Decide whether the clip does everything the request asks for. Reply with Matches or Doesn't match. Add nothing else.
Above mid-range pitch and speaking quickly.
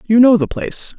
Matches